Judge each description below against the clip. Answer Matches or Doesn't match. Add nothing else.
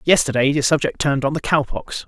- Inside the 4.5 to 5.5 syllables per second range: Doesn't match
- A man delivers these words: Matches